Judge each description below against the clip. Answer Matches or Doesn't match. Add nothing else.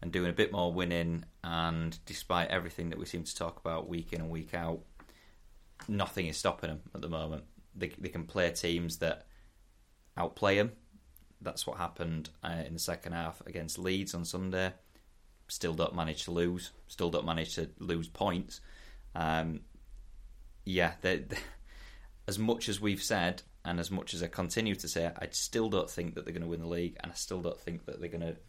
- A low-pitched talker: Matches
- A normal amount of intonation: Doesn't match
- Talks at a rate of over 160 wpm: Matches